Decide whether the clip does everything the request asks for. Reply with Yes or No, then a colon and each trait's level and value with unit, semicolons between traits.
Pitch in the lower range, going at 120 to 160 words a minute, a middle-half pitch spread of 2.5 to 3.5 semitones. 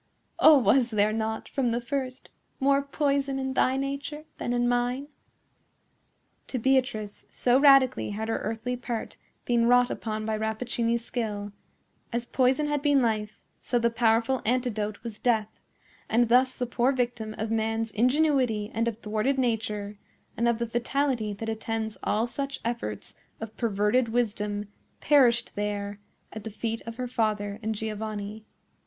No: high, 235 Hz; average, 150 wpm; average, 2.9 semitones